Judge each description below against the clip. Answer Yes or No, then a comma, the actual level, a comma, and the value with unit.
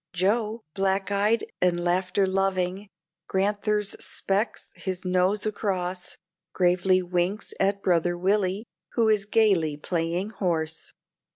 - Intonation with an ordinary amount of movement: No, narrow, 2.3 semitones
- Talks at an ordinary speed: No, slow, 110 wpm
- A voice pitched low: No, high, 190 Hz